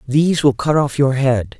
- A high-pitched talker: No, low, 135 Hz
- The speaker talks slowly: No, fast, 225 wpm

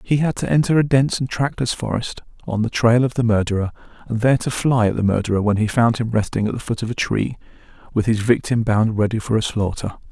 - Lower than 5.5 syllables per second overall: No, 6.1 syllables/s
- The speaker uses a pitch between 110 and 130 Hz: Yes, low, 115 Hz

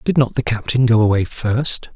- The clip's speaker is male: Yes, male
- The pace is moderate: No, fast, 215 wpm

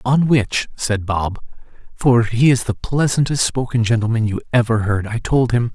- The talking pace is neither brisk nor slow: Yes, average, 175 wpm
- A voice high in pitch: No, low, 120 Hz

